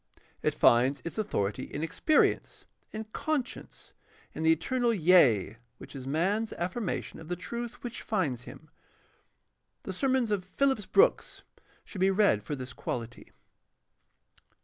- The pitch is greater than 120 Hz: Yes, medium, 185 Hz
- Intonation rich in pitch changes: Yes, wide, 8.5 semitones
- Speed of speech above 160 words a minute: No, slow, 135 wpm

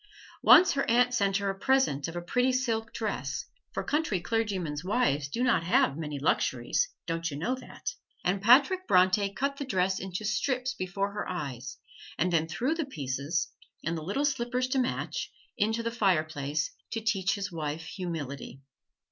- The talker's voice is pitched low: No, high, 195 Hz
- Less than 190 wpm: Yes, average, 175 wpm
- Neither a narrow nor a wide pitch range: No, wide, 7.1 semitones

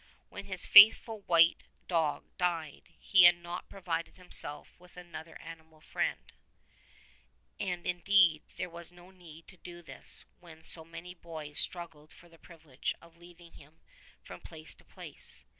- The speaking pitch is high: No, medium, 170 Hz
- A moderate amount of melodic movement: No, narrow, 1.7 semitones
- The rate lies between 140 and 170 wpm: Yes, average, 150 wpm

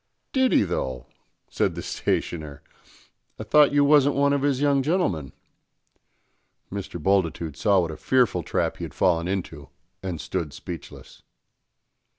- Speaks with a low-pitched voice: Yes, very low, 95 Hz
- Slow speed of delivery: No, average, 145 wpm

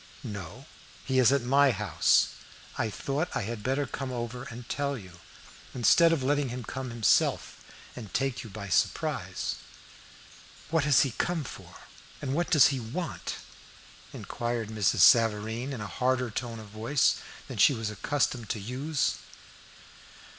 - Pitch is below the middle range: Yes, low, 125 Hz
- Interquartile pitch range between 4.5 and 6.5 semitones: No, average, 3.8 semitones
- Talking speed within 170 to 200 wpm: No, average, 155 wpm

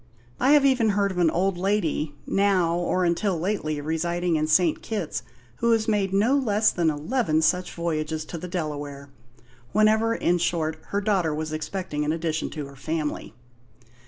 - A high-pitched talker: No, medium, 175 Hz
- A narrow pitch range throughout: No, average, 4.6 semitones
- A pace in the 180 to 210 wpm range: No, average, 170 wpm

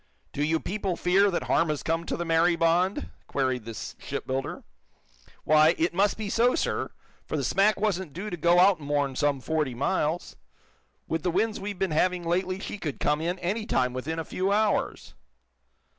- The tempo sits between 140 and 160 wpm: No, average, 190 wpm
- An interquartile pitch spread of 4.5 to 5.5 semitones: No, average, 4.0 semitones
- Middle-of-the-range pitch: Yes, medium, 170 Hz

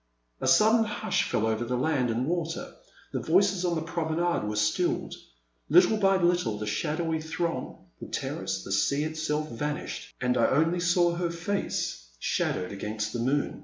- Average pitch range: No, wide, 6.7 semitones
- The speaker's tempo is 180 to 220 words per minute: No, average, 165 wpm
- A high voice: No, medium, 160 Hz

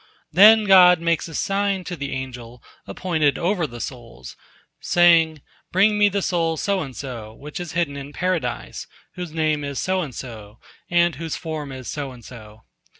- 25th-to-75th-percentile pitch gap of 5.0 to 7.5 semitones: Yes, wide, 5.4 semitones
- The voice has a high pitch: No, medium, 160 Hz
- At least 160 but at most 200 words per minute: Yes, average, 175 wpm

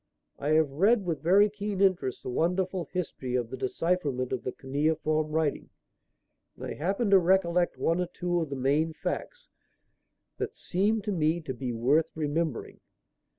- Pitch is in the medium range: Yes, medium, 160 Hz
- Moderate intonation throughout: Yes, average, 4.6 semitones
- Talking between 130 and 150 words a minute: No, average, 165 wpm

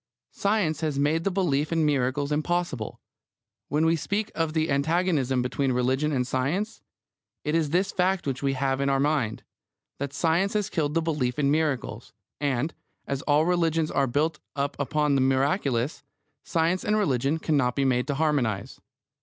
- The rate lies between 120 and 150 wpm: No, average, 170 wpm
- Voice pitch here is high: No, medium, 150 Hz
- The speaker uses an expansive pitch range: No, average, 3.3 semitones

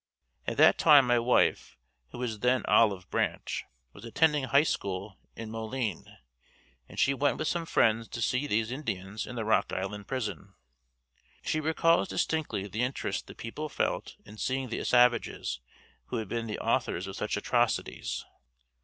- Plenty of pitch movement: No, average, 4.2 semitones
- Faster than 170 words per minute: No, average, 160 wpm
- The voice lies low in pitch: Yes, low, 115 Hz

